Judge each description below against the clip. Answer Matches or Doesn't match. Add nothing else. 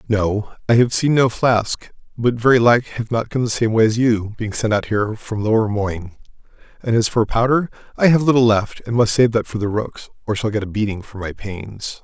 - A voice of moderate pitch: Doesn't match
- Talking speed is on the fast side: Matches